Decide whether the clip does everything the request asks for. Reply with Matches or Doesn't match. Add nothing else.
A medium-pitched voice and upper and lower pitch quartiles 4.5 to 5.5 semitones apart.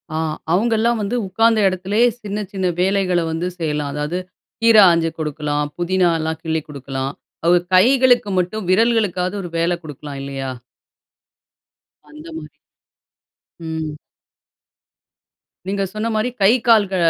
Matches